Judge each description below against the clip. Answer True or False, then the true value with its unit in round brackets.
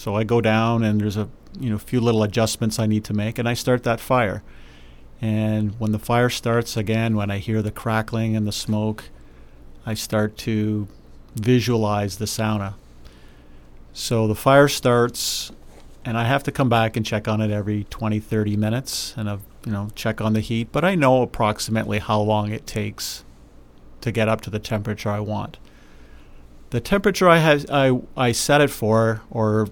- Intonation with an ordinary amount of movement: False (1.9 semitones)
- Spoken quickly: False (190 wpm)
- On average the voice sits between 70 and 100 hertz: False (110 Hz)